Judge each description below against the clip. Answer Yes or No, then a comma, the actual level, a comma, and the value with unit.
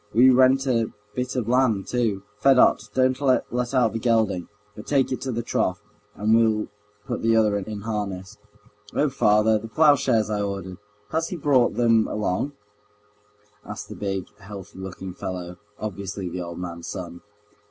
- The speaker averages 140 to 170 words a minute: Yes, average, 165 wpm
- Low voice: Yes, low, 110 Hz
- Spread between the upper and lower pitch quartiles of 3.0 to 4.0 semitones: No, average, 4.6 semitones